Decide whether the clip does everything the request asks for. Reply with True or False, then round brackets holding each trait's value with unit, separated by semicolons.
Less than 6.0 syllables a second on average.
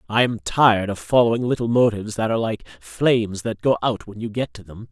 False (6.1 syllables/s)